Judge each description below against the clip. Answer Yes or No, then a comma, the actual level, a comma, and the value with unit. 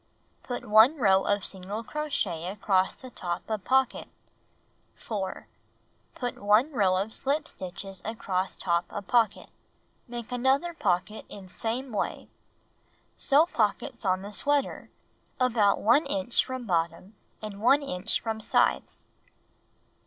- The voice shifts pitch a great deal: No, average, 4.9 semitones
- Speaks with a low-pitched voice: No, high, 215 Hz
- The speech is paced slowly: Yes, slow, 130 wpm